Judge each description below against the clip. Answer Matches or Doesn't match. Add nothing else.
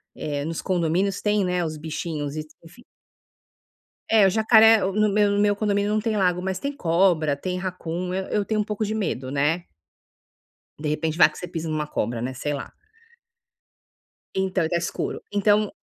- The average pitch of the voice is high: Doesn't match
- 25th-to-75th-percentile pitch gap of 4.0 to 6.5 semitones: Matches